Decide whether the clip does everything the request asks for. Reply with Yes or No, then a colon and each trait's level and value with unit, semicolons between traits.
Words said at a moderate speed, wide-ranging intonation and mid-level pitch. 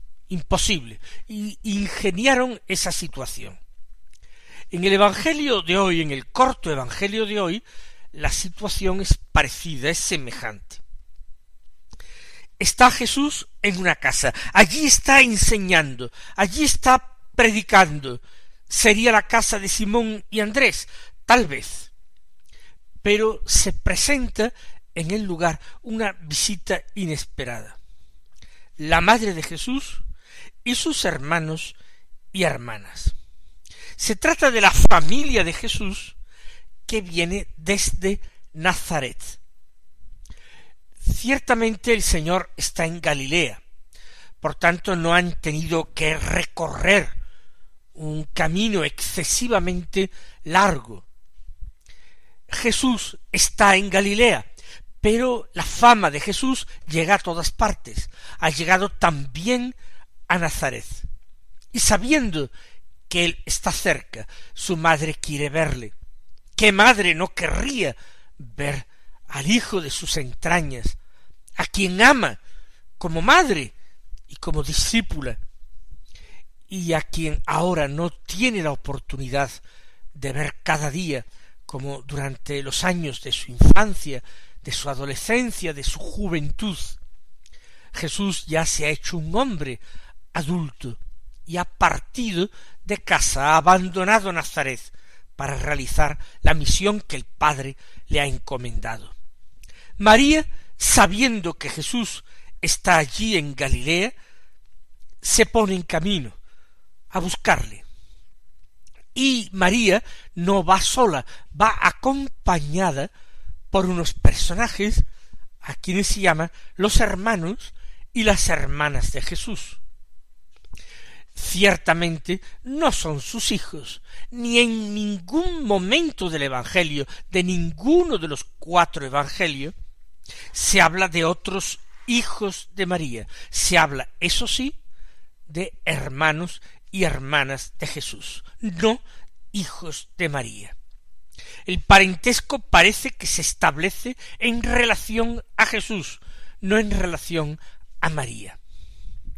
No: slow, 110 wpm; wide, 6.7 semitones; medium, 180 Hz